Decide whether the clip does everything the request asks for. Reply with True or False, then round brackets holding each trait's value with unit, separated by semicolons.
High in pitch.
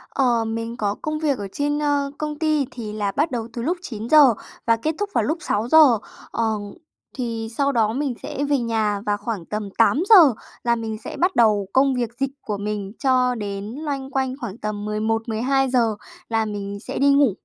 True (235 Hz)